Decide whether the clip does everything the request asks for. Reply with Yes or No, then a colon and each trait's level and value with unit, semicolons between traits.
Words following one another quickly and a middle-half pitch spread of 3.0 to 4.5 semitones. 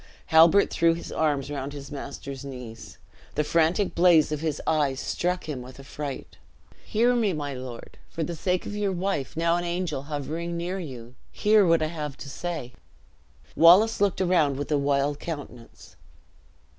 No: average, 170 wpm; average, 3.8 semitones